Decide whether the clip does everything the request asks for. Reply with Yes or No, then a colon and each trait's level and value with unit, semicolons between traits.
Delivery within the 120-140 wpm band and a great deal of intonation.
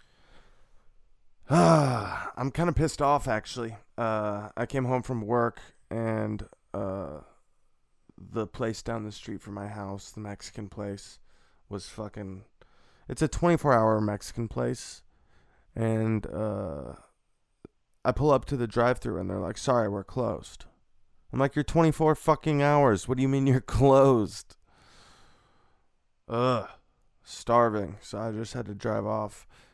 No: slow, 135 wpm; average, 4.2 semitones